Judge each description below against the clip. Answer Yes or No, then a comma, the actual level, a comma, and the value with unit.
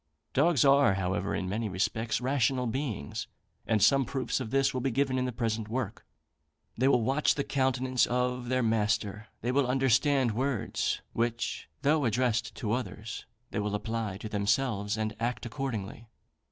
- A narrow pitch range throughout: No, average, 3.4 semitones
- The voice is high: No, low, 120 Hz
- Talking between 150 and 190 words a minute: Yes, average, 165 wpm